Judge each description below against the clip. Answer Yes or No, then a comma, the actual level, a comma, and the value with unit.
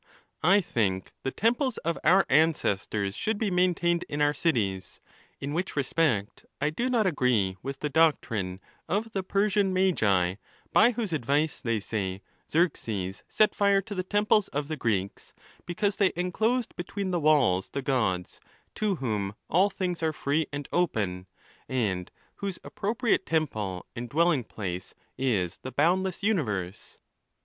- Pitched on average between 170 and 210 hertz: No, medium, 155 Hz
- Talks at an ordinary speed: Yes, average, 150 wpm